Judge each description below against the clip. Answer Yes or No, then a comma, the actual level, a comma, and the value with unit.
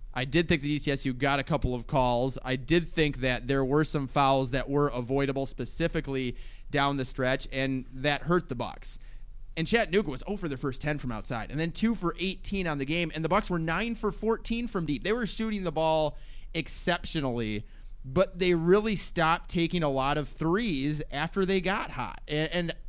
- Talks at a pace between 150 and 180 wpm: No, fast, 205 wpm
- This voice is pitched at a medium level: Yes, medium, 150 Hz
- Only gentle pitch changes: No, average, 4.6 semitones